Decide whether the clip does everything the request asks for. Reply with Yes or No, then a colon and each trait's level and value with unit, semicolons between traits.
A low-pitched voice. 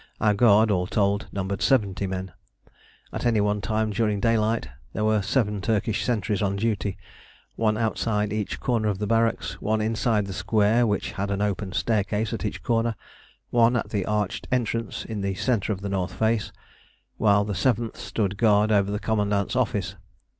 Yes: low, 105 Hz